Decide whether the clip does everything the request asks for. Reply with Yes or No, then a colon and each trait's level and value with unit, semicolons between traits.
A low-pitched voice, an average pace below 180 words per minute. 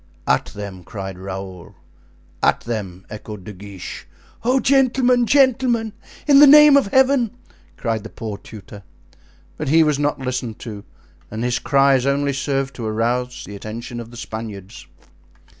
Yes: low, 125 Hz; average, 150 wpm